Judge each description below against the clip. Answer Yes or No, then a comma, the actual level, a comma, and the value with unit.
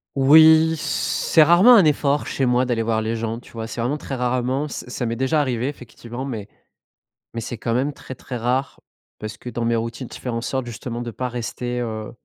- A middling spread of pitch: Yes, average, 3.0 semitones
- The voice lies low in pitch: Yes, low, 125 Hz